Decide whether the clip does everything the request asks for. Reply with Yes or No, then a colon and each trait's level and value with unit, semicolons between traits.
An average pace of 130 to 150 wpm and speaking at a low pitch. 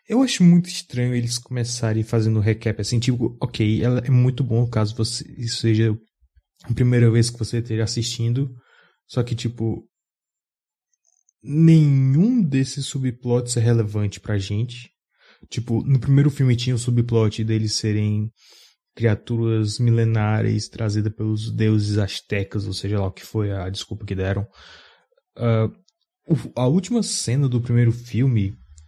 Yes: average, 140 wpm; low, 115 Hz